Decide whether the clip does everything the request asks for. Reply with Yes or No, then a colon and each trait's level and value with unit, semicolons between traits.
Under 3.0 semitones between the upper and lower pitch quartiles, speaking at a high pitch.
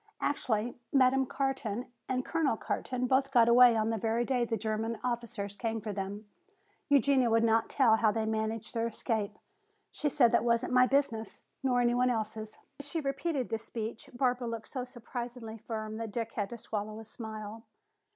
Yes: narrow, 2.4 semitones; high, 230 Hz